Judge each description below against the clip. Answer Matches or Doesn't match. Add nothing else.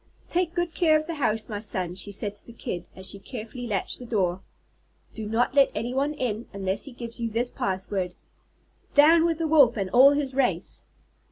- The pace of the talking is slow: Doesn't match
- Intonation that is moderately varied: Doesn't match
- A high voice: Matches